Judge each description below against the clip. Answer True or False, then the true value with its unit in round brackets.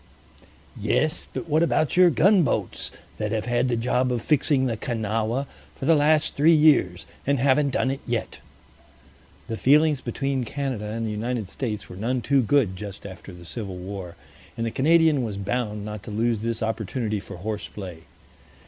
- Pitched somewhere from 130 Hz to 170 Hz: False (120 Hz)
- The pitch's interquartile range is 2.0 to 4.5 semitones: False (4.9 semitones)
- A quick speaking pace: False (175 wpm)